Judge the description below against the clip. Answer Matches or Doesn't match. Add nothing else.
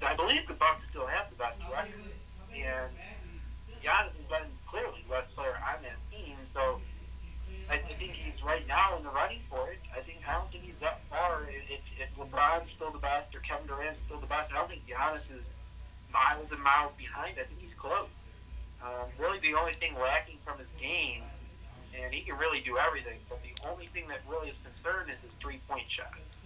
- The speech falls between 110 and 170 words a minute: Doesn't match